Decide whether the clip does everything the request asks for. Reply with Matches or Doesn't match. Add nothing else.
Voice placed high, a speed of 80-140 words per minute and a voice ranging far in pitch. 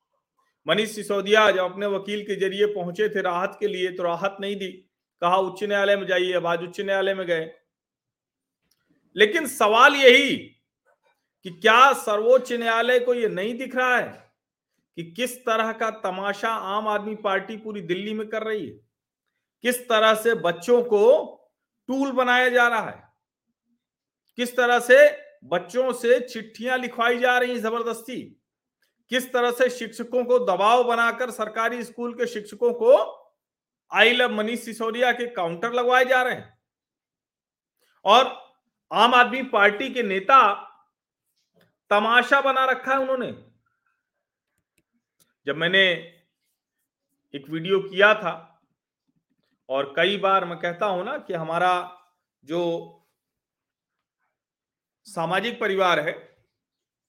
Doesn't match